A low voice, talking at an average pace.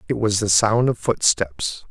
Yes: low, 105 Hz; average, 190 wpm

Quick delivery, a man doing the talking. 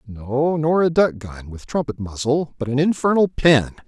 No: average, 185 wpm; male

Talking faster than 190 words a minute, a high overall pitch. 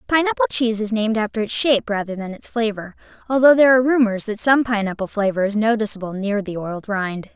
Yes: fast, 205 wpm; high, 220 Hz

